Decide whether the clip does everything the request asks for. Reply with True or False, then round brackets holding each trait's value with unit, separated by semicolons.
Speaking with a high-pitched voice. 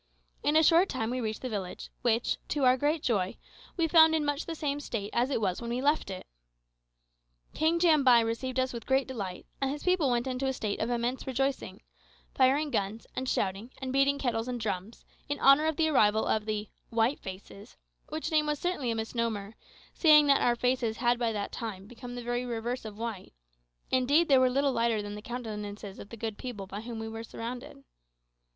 True (245 Hz)